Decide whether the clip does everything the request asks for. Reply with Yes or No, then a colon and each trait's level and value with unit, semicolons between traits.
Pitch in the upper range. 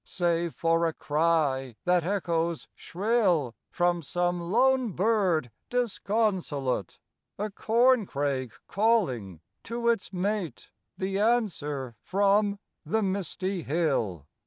No: medium, 175 Hz